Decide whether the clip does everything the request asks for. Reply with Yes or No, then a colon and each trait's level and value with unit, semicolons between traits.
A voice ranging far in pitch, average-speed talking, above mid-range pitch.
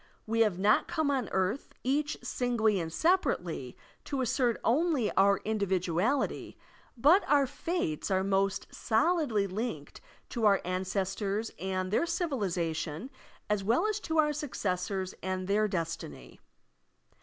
No: wide, 6.6 semitones; slow, 130 wpm; high, 210 Hz